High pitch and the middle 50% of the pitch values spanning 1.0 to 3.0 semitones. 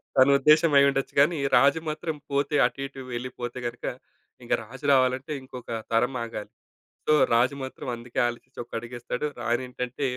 No: low, 130 Hz; narrow, 2.6 semitones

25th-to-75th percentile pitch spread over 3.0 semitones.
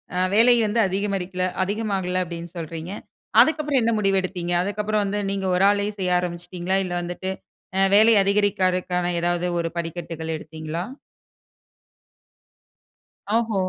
No: average, 2.7 semitones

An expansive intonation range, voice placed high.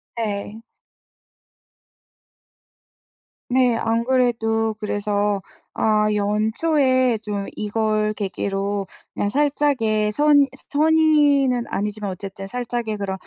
No: average, 3.9 semitones; high, 220 Hz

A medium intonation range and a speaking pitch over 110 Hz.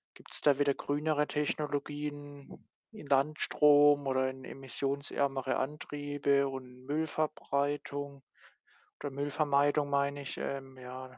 No: narrow, 1.2 semitones; medium, 140 Hz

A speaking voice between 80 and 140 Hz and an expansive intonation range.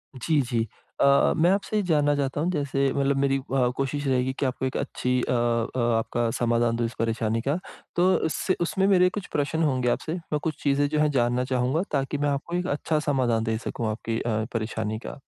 No: low, 135 Hz; average, 4.1 semitones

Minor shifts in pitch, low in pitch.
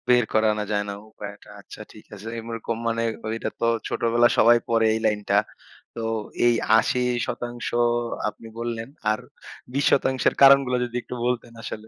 Yes: narrow, 1.9 semitones; low, 115 Hz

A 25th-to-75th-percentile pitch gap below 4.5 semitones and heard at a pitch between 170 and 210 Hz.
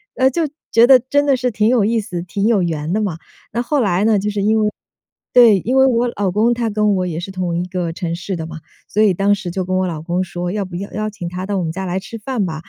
Yes: average, 4.1 semitones; high, 200 Hz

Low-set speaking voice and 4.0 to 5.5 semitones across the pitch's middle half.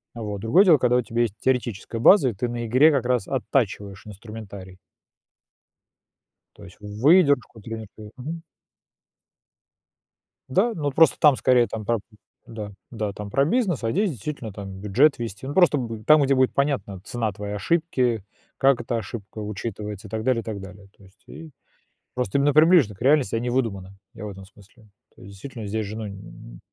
Yes: low, 115 Hz; average, 4.7 semitones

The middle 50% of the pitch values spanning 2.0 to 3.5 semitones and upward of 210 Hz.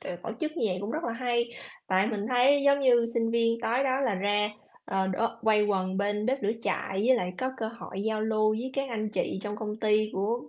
Yes: average, 2.9 semitones; high, 220 Hz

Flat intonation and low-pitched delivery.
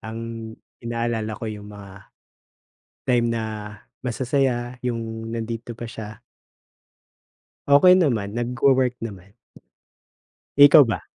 Yes: narrow, 2.0 semitones; low, 115 Hz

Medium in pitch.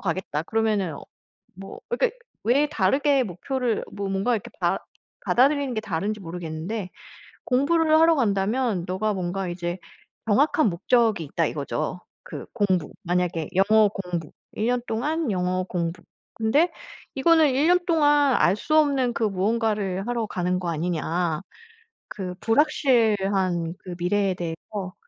No: high, 205 Hz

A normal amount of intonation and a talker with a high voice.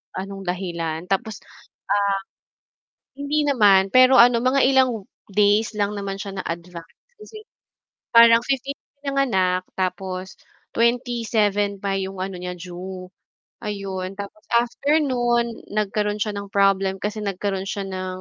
Yes: average, 3.7 semitones; high, 200 Hz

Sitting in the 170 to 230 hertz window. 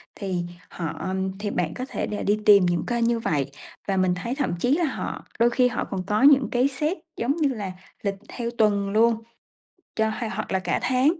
Yes: high, 220 Hz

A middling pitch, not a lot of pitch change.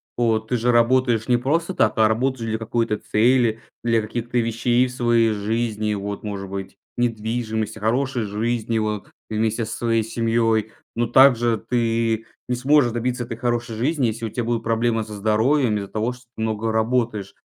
No: low, 115 Hz; narrow, 1.7 semitones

